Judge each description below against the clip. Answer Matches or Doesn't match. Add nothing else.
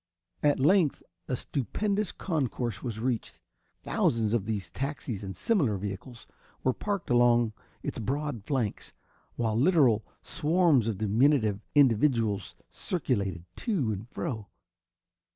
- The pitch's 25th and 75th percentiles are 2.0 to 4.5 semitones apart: Doesn't match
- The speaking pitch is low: Matches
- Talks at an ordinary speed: Doesn't match